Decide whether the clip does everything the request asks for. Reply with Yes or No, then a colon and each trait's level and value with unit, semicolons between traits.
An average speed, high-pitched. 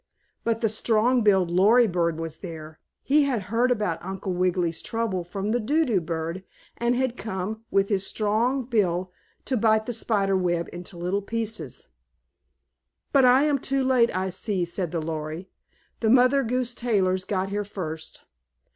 Yes: average, 165 wpm; high, 205 Hz